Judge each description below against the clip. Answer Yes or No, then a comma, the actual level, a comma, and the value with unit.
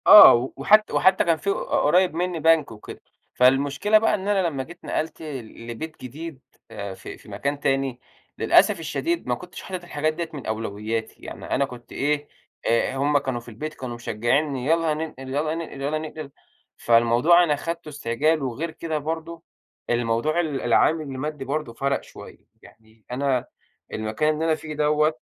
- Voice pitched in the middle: Yes, medium, 145 Hz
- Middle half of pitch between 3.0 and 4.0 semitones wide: No, average, 4.5 semitones